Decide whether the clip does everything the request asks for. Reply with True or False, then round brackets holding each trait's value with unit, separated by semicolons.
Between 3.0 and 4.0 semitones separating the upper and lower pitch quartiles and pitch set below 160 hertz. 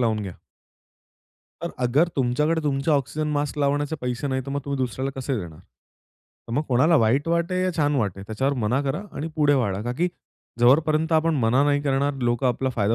True (3.6 semitones; 140 Hz)